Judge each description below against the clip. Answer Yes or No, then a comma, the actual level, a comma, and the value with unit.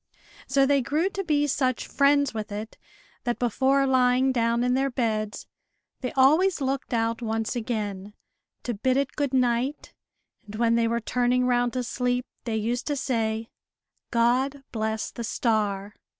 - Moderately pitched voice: No, high, 245 Hz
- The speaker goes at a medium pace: Yes, average, 160 wpm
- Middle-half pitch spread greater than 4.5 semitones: No, average, 2.9 semitones